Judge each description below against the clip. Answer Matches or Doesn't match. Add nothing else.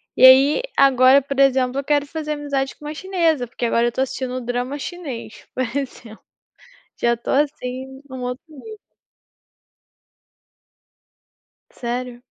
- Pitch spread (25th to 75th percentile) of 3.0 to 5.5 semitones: Doesn't match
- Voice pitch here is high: Matches